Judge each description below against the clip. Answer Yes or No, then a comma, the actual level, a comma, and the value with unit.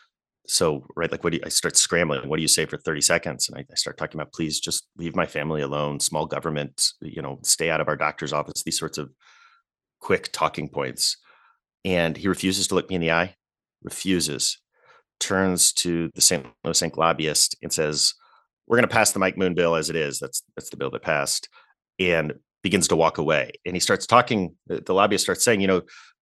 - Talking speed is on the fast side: Yes, fast, 220 wpm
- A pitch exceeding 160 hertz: No, very low, 85 Hz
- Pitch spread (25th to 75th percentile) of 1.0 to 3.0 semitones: No, average, 4.0 semitones